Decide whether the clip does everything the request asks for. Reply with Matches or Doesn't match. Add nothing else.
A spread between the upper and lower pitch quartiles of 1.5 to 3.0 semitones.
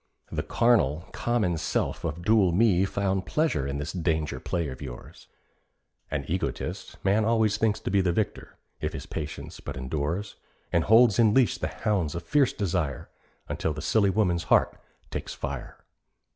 Doesn't match